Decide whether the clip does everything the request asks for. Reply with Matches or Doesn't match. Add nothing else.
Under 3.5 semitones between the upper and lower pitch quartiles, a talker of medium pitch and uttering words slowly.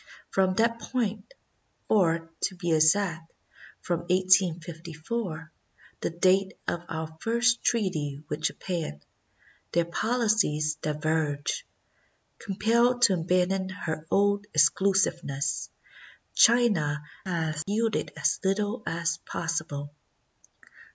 Doesn't match